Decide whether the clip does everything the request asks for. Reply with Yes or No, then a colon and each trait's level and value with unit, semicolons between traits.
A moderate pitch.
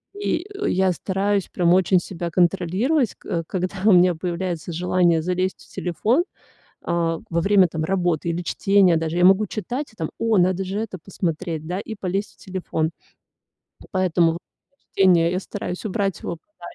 Yes: medium, 180 Hz